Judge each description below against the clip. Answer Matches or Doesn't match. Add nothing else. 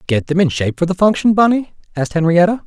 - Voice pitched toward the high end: Doesn't match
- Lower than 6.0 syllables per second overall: Doesn't match